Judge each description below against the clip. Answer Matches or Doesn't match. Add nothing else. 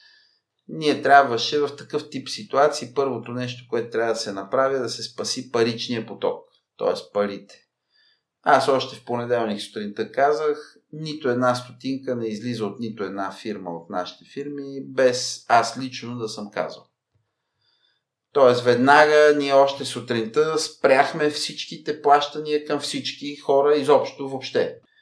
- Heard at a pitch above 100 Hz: Matches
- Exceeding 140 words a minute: Doesn't match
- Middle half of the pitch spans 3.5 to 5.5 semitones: Matches